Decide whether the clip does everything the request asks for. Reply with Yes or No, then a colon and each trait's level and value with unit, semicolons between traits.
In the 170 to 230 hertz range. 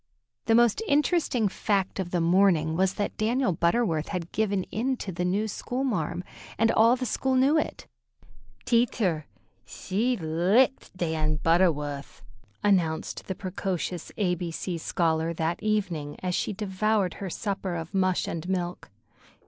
Yes: medium, 185 Hz